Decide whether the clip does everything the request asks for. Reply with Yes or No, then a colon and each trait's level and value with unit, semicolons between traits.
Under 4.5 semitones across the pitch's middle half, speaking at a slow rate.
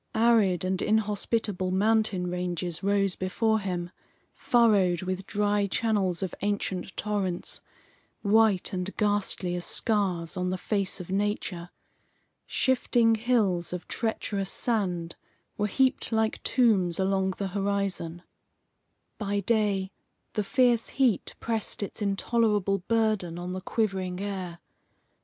Yes: average, 3.0 semitones; slow, 120 wpm